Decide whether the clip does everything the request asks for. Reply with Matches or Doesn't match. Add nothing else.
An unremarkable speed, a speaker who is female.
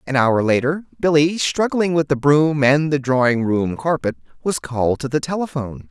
Doesn't match